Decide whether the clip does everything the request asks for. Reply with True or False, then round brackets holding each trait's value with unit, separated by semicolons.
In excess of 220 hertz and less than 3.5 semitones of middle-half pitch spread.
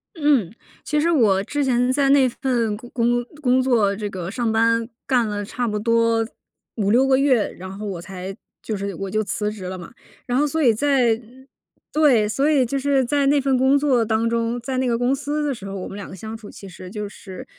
False (230 Hz; 4.3 semitones)